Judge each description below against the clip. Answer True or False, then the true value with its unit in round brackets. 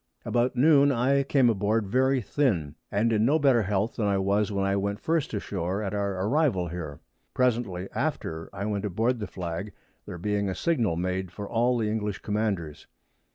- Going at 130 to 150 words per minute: False (185 wpm)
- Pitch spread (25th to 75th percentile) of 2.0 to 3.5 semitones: False (4.2 semitones)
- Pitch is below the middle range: True (105 Hz)